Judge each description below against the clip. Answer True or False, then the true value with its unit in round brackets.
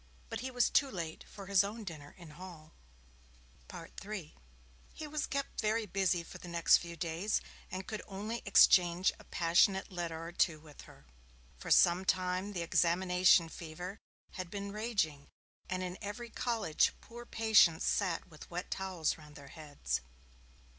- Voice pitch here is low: False (185 Hz)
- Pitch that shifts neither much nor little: True (3.6 semitones)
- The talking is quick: False (160 wpm)